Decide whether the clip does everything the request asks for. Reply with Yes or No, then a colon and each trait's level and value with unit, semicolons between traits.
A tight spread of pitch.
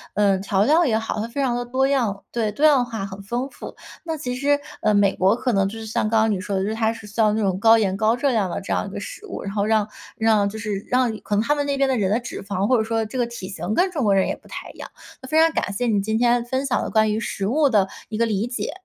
No: average, 3.5 semitones